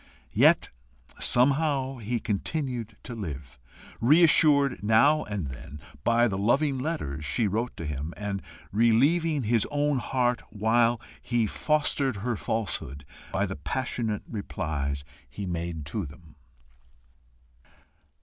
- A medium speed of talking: No, slow, 120 wpm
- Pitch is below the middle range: Yes, low, 115 Hz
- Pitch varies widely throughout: Yes, wide, 6.6 semitones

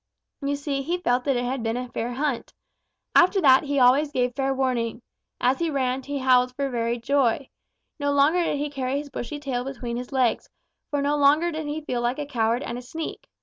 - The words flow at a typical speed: No, fast, 220 wpm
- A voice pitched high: Yes, very high, 270 Hz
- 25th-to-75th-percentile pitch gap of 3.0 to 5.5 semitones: No, narrow, 2.6 semitones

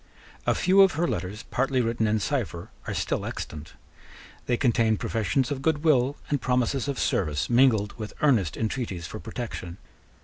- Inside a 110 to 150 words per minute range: No, average, 165 wpm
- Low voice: Yes, low, 120 Hz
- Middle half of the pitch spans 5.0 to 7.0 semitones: No, average, 4.4 semitones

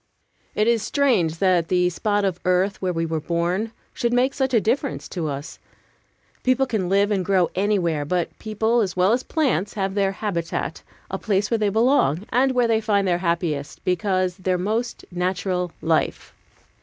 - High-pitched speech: Yes, high, 195 Hz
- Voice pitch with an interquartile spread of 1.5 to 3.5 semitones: No, average, 3.9 semitones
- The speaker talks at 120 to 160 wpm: No, average, 180 wpm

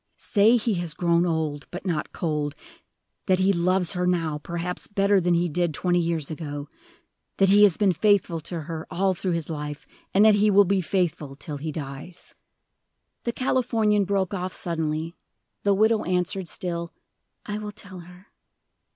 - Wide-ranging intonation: No, average, 3.5 semitones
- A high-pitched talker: No, medium, 180 Hz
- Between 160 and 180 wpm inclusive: Yes, average, 170 wpm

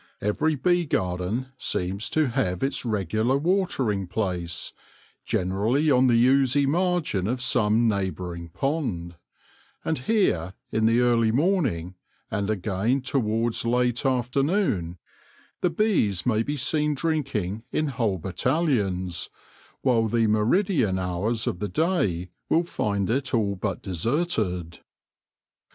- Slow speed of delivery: Yes, slow, 125 wpm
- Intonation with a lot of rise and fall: Yes, wide, 6.5 semitones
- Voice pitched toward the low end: Yes, low, 115 Hz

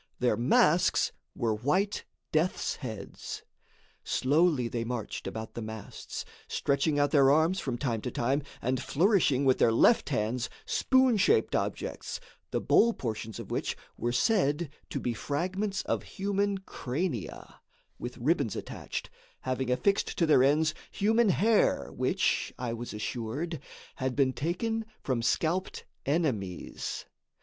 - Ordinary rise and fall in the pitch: No, wide, 6.9 semitones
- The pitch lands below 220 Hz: Yes, medium, 140 Hz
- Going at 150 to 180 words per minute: No, slow, 135 wpm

